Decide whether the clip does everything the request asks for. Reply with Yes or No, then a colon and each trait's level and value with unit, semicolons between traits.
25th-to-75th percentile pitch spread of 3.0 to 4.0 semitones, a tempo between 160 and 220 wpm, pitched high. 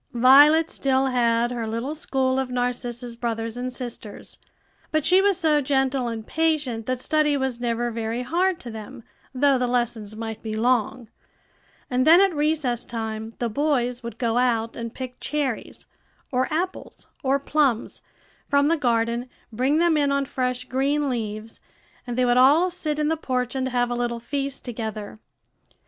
Yes: average, 3.4 semitones; average, 170 wpm; very high, 250 Hz